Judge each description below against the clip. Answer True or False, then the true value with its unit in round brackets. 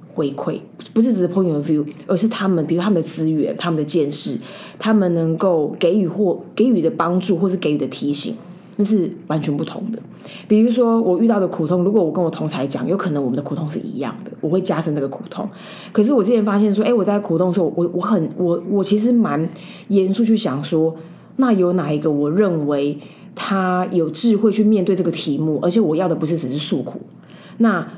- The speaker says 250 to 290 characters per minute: False (335 characters per minute)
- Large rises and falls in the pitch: False (4.4 semitones)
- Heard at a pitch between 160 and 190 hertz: True (185 Hz)